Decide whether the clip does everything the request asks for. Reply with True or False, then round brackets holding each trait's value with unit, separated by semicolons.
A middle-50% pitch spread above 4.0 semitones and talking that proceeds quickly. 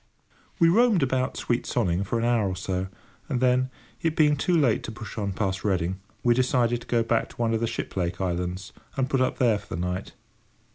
True (5.3 semitones; 220 wpm)